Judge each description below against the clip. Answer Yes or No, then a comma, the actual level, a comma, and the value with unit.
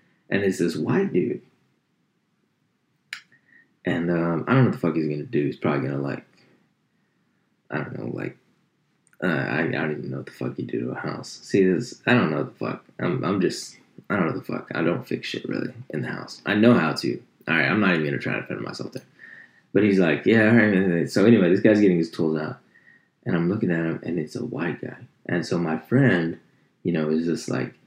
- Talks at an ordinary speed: No, fast, 240 wpm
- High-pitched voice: No, very low, 85 Hz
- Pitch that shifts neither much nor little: Yes, average, 3.2 semitones